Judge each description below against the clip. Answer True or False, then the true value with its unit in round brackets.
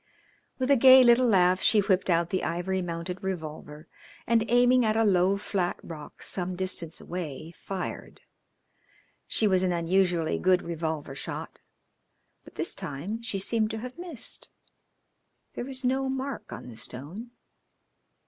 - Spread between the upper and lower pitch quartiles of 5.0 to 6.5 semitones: True (5.3 semitones)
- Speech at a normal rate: True (150 wpm)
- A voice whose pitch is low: False (190 Hz)